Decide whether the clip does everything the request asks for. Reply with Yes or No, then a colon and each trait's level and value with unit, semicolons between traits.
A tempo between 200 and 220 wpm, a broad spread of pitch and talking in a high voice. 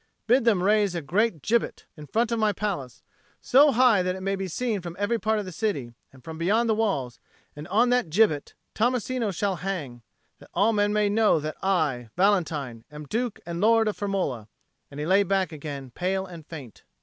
Yes: fast, 205 wpm; wide, 5.8 semitones; high, 195 Hz